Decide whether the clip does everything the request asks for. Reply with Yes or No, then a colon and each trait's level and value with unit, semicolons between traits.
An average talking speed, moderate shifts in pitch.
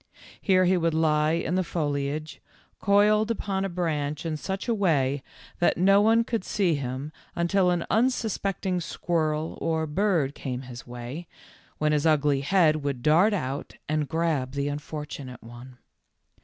Yes: average, 160 wpm; average, 4.7 semitones